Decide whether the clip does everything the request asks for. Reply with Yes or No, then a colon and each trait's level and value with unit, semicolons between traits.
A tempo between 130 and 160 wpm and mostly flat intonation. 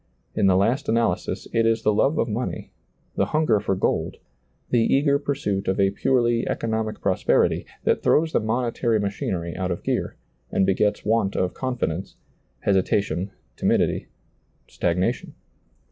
No: average, 145 wpm; average, 3.6 semitones